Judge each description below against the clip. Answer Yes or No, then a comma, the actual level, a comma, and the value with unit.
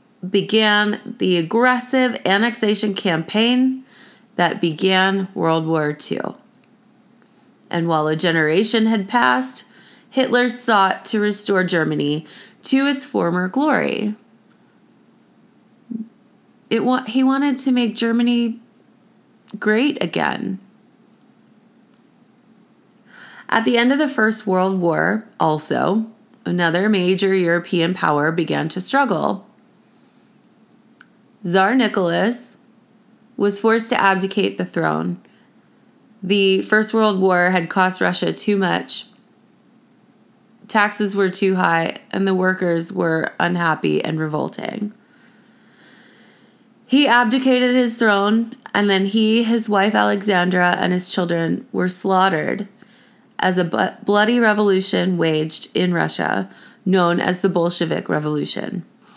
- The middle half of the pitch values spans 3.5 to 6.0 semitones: Yes, average, 4.2 semitones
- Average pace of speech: No, slow, 105 wpm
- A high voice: Yes, high, 215 Hz